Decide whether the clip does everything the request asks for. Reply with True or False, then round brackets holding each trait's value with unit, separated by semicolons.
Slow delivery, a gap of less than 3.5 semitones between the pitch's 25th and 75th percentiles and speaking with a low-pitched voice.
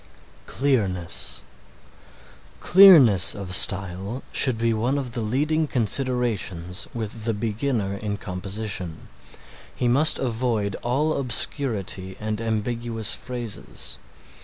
False (100 wpm; 4.3 semitones; 110 Hz)